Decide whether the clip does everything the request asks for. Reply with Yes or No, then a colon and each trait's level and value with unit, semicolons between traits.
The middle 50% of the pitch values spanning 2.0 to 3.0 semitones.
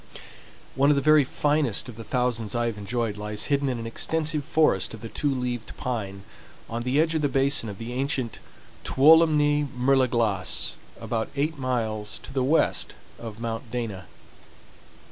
No: average, 4.0 semitones